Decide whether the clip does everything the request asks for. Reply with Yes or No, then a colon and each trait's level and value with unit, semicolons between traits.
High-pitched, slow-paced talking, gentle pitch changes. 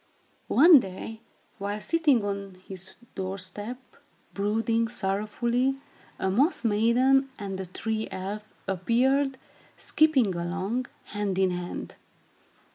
No: high, 210 Hz; slow, 110 wpm; average, 4.6 semitones